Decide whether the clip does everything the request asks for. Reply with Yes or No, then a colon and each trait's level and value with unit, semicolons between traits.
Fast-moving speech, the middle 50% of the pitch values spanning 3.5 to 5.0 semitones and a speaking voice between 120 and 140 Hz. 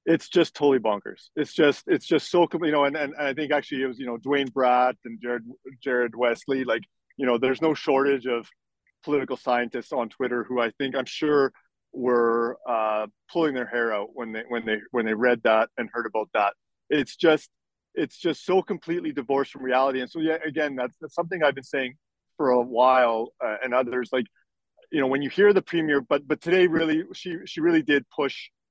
Yes: fast, 215 wpm; average, 4.0 semitones; low, 135 Hz